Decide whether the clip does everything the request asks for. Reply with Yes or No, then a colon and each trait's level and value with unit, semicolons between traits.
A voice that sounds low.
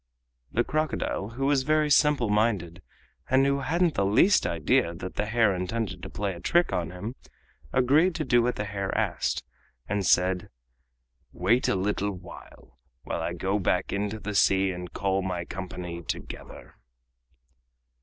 Yes: low, 105 Hz